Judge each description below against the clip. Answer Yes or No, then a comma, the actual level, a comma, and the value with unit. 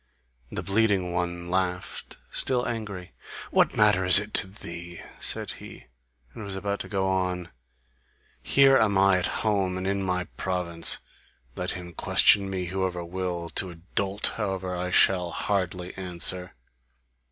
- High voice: No, very low, 95 Hz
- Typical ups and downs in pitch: No, narrow, 1.7 semitones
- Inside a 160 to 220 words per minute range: No, average, 150 wpm